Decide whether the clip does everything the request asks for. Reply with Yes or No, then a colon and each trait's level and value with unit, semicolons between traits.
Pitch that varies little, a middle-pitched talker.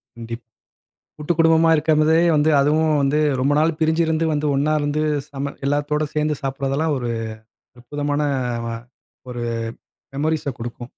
Yes: narrow, 2.3 semitones; medium, 150 Hz